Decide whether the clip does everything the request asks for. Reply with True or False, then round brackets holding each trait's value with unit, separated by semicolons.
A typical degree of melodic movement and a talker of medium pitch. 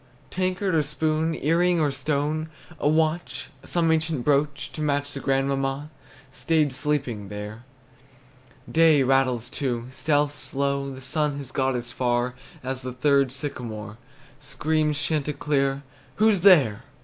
True (3.0 semitones; 145 Hz)